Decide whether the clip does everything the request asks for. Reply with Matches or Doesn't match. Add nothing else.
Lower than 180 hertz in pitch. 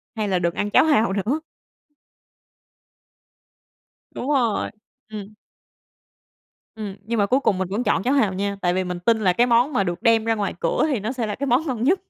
Doesn't match